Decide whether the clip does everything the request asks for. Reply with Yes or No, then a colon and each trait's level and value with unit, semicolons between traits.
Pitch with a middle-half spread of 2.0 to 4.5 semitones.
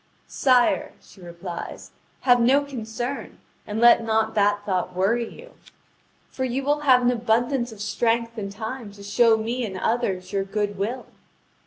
Yes: average, 3.3 semitones